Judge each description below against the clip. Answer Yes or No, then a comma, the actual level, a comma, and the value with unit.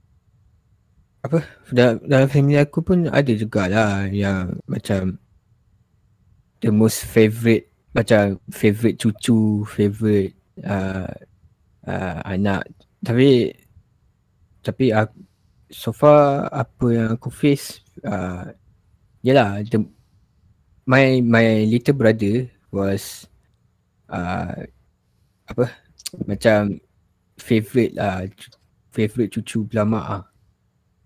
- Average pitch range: Yes, average, 3.1 semitones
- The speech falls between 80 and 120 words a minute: Yes, slow, 90 wpm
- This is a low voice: Yes, low, 110 Hz